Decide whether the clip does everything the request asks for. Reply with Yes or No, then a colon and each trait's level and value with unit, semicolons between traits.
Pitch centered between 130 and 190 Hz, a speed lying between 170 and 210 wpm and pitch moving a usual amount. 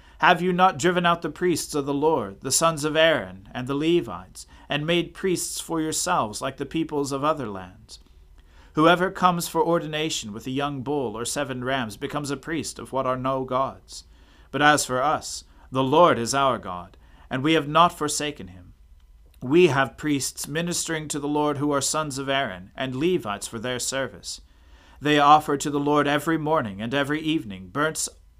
No: medium, 140 Hz; average, 190 wpm; wide, 5.9 semitones